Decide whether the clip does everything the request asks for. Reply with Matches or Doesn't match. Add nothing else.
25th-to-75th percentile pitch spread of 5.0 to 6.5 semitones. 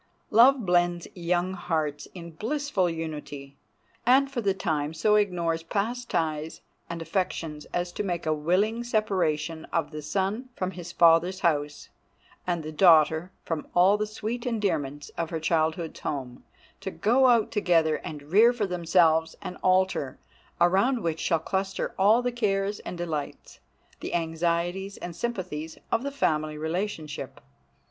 Doesn't match